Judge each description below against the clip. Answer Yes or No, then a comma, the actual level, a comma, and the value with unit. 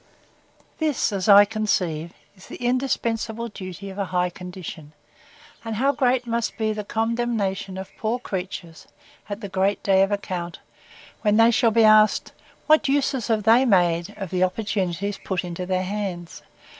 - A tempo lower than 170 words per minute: Yes, average, 160 wpm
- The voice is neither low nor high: No, high, 205 Hz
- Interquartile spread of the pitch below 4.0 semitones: Yes, average, 3.6 semitones